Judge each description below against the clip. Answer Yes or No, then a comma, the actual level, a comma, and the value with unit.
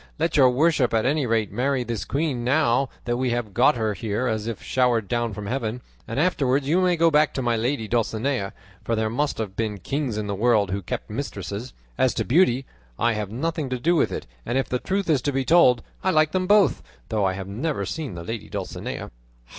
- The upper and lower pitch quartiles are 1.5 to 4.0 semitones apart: No, average, 4.7 semitones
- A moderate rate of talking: No, fast, 225 wpm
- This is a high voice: No, low, 125 Hz